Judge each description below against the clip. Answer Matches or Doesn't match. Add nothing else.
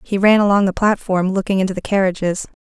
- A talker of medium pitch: Doesn't match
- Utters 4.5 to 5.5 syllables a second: Doesn't match